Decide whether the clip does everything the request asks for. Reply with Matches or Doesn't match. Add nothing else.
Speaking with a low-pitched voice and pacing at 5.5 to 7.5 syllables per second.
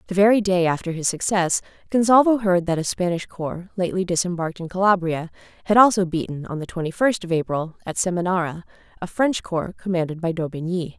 Doesn't match